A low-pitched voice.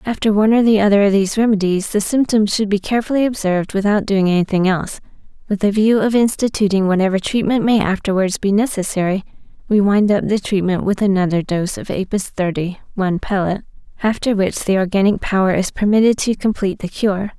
No: high, 200 Hz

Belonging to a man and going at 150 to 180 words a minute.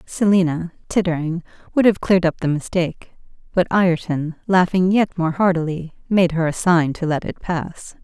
No: female; average, 165 wpm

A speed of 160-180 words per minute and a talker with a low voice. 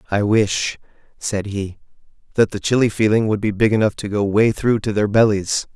No: average, 200 wpm; low, 105 Hz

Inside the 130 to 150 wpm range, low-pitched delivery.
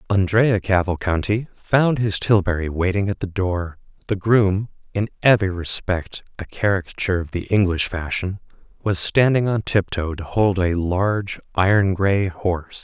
Yes: average, 145 wpm; very low, 95 Hz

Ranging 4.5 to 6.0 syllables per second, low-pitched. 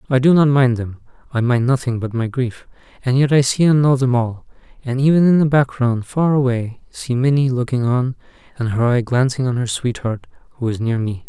Yes: 5.3 syllables/s; low, 125 Hz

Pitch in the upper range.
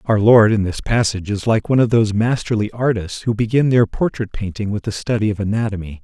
No: low, 110 Hz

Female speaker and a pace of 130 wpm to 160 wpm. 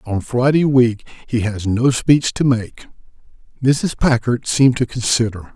No: male; average, 150 wpm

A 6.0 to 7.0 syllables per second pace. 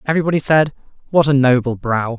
Yes: 6.5 syllables/s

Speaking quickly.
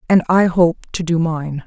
Yes: fast, 215 wpm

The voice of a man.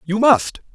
Yes: male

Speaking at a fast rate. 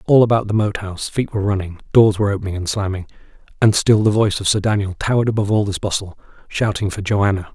Yes: fast, 225 wpm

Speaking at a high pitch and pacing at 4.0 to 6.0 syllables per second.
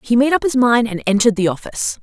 No: high, 235 Hz; 7.0 syllables/s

